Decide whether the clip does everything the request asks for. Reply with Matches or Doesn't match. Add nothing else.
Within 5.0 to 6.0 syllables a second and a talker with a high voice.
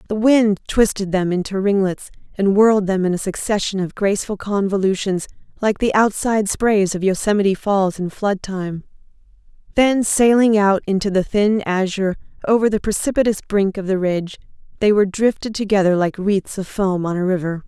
Matches